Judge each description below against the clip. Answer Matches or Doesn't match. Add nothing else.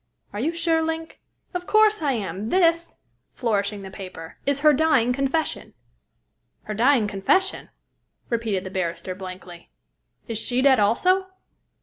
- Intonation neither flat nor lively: Doesn't match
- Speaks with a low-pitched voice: Doesn't match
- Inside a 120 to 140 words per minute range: Matches